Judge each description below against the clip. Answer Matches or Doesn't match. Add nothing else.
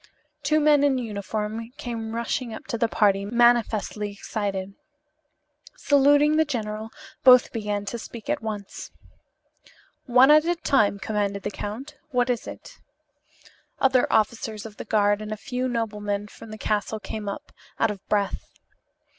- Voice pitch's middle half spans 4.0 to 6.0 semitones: Doesn't match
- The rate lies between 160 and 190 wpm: Doesn't match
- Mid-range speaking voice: Doesn't match